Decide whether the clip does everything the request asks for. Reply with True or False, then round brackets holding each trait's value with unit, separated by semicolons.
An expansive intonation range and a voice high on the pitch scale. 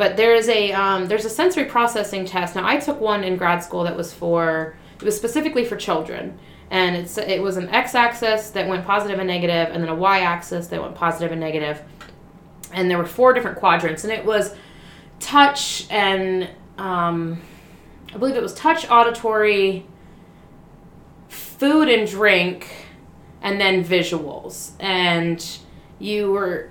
False (4.0 semitones; 195 Hz)